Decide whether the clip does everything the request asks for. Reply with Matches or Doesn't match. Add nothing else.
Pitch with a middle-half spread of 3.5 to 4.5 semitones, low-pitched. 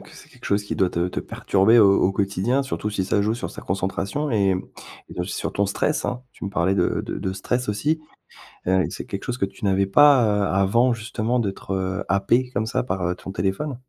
Matches